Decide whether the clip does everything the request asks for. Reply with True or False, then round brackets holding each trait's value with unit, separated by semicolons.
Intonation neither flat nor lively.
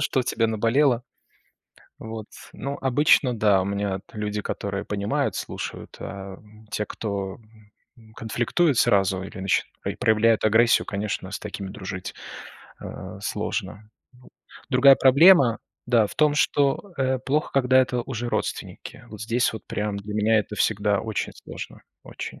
True (4.0 semitones)